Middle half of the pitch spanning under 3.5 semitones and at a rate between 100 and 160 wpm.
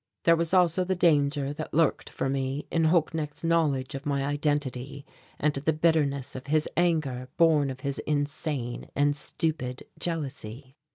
Yes: average, 2.8 semitones; average, 155 wpm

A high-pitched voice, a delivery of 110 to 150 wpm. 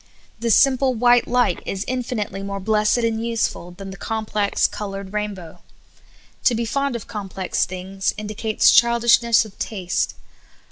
Yes: high, 215 Hz; average, 145 wpm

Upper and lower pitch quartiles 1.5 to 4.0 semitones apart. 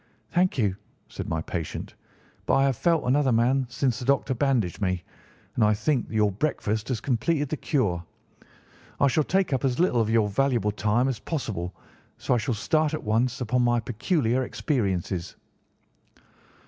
No: average, 4.5 semitones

